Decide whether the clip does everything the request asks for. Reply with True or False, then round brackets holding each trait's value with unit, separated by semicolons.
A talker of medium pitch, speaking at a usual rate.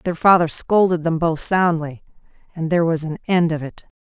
True (165 Hz; 195 wpm)